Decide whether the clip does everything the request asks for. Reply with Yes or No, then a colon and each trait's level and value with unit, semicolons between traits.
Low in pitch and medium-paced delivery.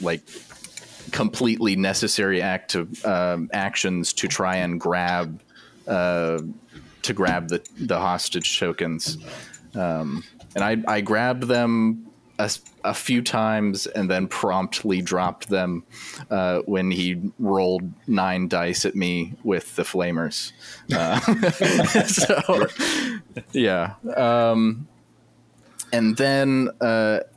No: very low, 95 Hz; slow, 110 wpm